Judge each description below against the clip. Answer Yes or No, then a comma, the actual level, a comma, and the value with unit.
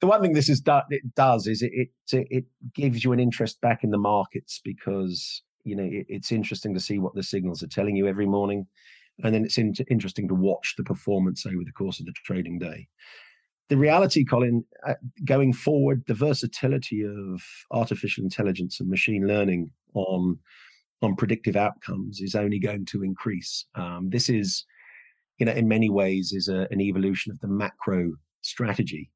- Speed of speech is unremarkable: Yes, average, 180 wpm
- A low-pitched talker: Yes, low, 105 Hz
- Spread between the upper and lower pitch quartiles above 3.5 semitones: Yes, average, 4.2 semitones